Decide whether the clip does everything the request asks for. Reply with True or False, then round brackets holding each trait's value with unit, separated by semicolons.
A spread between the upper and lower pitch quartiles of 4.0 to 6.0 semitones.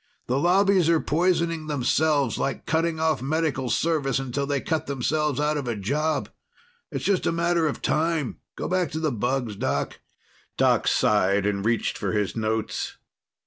True (4.7 semitones)